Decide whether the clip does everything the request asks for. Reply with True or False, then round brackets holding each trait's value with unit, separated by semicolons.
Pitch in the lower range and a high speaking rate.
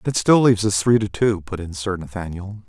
True (100 Hz; 245 wpm)